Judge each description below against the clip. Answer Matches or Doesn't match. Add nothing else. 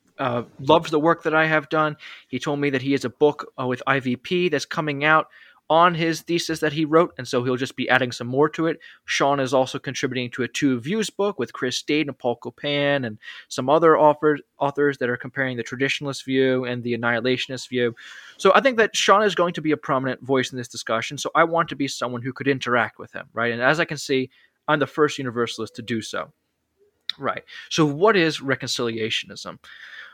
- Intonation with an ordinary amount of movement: Matches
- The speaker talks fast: Matches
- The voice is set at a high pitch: Doesn't match